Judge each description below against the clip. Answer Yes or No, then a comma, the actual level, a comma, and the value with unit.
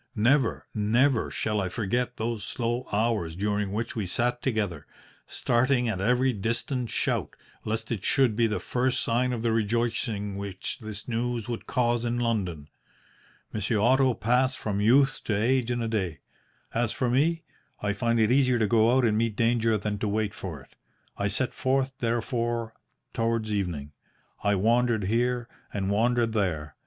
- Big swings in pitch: No, average, 2.8 semitones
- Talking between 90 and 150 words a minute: No, average, 170 wpm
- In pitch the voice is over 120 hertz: No, low, 115 Hz